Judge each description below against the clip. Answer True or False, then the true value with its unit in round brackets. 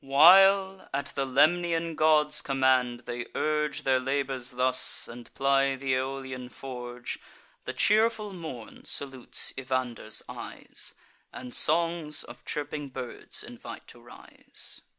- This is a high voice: False (135 Hz)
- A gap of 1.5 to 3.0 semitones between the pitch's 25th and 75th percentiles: False (3.4 semitones)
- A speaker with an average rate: False (120 wpm)